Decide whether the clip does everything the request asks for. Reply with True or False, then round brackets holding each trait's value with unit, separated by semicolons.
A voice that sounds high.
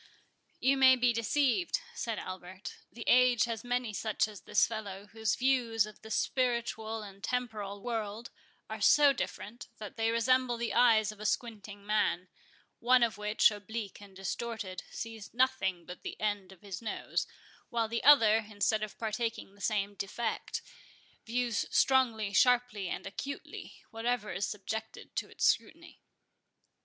True (220 Hz)